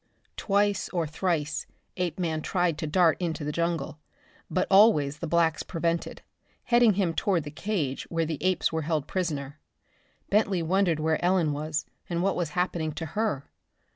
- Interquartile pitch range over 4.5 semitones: No, average, 3.1 semitones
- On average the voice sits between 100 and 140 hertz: No, medium, 170 Hz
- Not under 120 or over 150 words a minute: No, average, 160 wpm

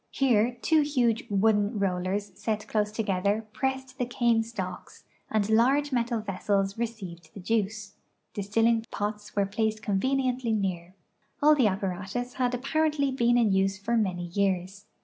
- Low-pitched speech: No, high, 215 Hz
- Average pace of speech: Yes, average, 150 wpm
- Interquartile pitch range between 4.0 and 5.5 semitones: No, average, 3.6 semitones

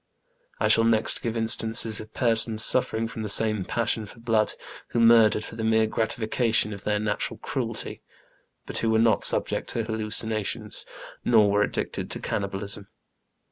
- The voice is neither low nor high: No, low, 110 Hz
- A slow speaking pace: No, average, 165 wpm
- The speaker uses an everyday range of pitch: No, narrow, 1.1 semitones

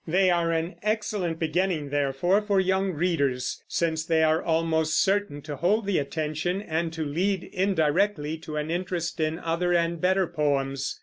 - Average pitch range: Yes, average, 3.1 semitones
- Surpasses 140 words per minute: Yes, average, 165 wpm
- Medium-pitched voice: Yes, medium, 165 Hz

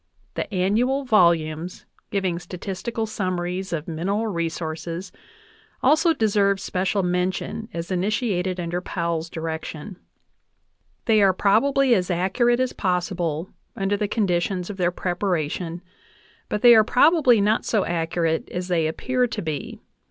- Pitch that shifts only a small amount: No, average, 3.8 semitones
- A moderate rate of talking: No, slow, 130 wpm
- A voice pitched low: No, medium, 185 Hz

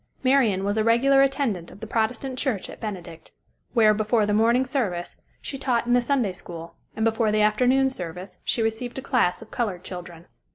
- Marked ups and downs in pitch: No, average, 4.7 semitones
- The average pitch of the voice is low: No, high, 220 Hz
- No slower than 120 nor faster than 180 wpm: No, average, 195 wpm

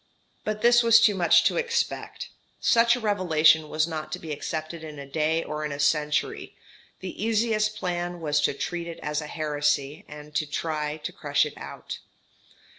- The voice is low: No, medium, 160 Hz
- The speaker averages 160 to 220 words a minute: Yes, average, 180 wpm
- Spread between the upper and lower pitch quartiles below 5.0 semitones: No, average, 5.3 semitones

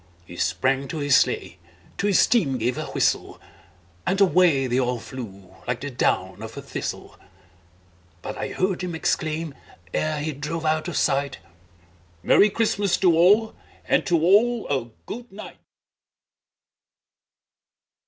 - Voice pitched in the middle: Yes, medium, 155 Hz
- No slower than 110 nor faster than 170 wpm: Yes, average, 145 wpm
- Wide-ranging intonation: Yes, wide, 6.1 semitones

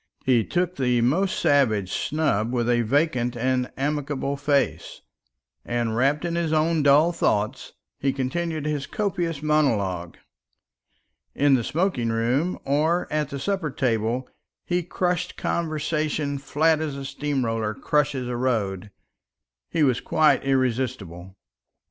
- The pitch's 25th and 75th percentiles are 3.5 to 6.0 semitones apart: Yes, average, 4.4 semitones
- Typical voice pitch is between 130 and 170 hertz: Yes, medium, 140 Hz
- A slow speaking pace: Yes, slow, 130 wpm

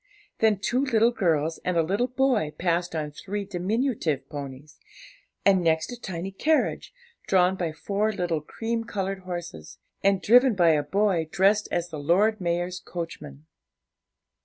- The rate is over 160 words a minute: No, average, 150 wpm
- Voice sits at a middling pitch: Yes, medium, 180 Hz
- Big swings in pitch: No, average, 4.6 semitones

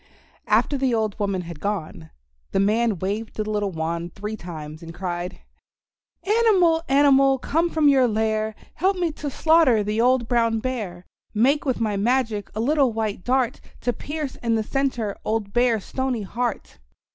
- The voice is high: Yes, high, 225 Hz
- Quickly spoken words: No, average, 165 wpm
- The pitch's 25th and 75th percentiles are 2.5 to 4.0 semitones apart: No, average, 4.8 semitones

